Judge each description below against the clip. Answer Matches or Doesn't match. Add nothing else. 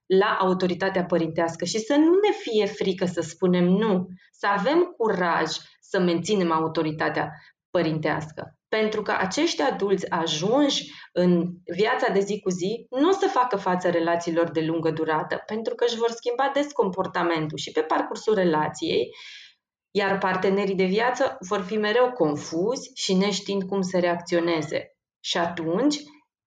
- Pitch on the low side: Doesn't match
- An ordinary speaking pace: Matches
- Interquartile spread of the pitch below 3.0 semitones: Doesn't match